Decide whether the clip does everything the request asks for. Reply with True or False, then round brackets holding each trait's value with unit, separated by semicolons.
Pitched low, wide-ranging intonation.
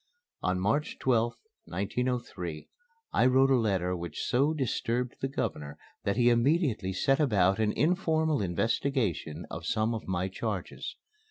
True (115 Hz; 6.2 semitones)